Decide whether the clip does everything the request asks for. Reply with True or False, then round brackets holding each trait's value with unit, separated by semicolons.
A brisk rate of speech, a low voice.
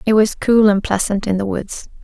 False (235 wpm; 205 Hz)